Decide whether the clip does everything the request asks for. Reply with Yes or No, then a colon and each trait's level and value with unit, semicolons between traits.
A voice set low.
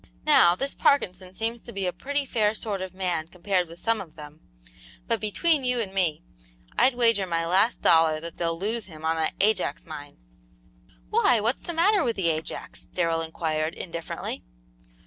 No: medium, 185 Hz